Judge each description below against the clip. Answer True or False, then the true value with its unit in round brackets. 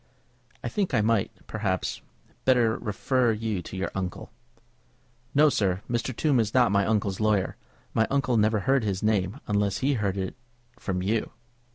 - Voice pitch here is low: True (110 Hz)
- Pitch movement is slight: False (3.6 semitones)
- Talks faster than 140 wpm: True (170 wpm)